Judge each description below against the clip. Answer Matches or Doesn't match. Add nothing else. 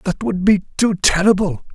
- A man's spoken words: Matches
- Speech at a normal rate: Matches